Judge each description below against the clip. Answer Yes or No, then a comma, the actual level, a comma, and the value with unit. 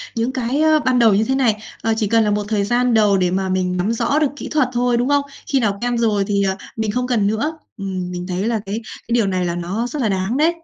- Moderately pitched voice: No, high, 220 Hz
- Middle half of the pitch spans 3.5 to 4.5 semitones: Yes, average, 4.0 semitones